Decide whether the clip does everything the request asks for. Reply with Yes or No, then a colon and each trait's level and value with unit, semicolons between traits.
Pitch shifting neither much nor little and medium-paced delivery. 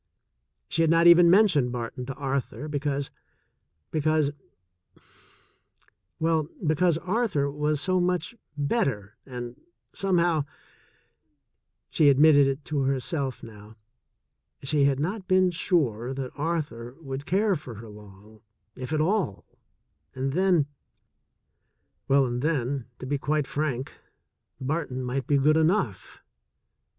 No: average, 4.2 semitones; slow, 130 wpm